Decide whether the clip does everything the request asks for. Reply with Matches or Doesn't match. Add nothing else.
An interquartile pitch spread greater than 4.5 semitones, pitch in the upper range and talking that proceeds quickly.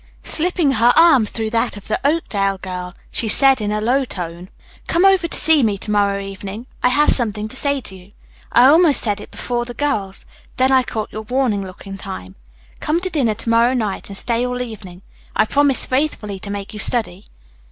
Matches